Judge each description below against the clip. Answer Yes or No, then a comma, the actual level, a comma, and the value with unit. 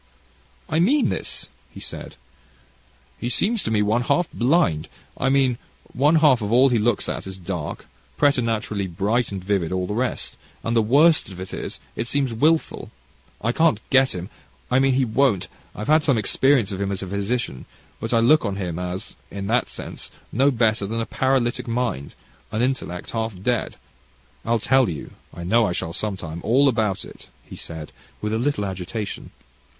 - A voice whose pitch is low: Yes, low, 115 Hz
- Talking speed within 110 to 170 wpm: No, average, 185 wpm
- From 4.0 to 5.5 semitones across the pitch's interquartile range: Yes, average, 5.1 semitones